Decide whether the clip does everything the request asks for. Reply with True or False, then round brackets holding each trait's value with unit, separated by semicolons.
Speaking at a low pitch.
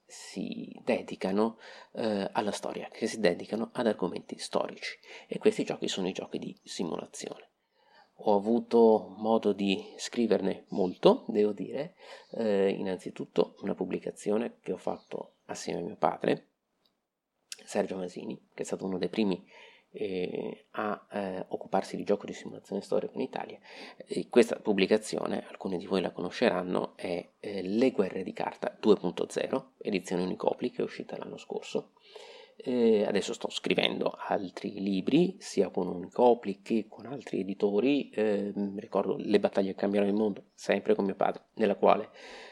True (105 Hz)